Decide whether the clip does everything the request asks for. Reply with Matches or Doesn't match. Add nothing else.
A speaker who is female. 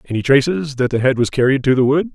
Doesn't match